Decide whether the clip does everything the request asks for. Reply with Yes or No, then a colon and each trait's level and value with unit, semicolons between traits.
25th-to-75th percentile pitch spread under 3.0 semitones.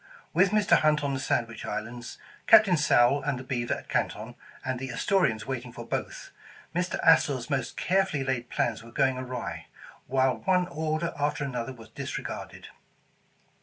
No: average, 4.4 semitones